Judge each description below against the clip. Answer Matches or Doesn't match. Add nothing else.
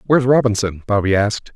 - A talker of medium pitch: Doesn't match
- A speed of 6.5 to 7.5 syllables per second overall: Matches